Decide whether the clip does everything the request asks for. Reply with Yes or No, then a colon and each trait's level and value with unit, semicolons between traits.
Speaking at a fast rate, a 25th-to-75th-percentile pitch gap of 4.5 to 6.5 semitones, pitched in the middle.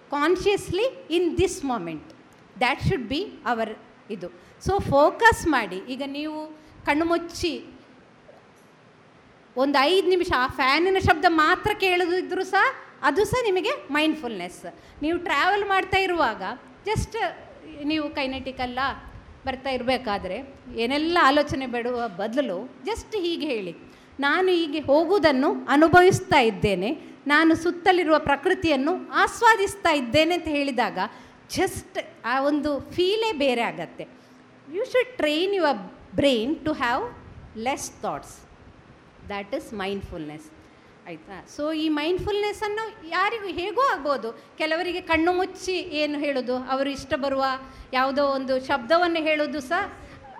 No: fast, 115 wpm; wide, 5.4 semitones; very high, 305 Hz